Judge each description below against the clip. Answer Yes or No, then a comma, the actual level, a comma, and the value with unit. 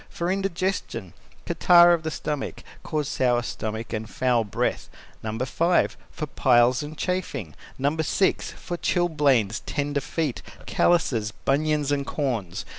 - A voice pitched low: No, medium, 145 Hz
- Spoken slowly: Yes, slow, 130 wpm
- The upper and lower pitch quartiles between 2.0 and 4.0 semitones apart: No, wide, 5.6 semitones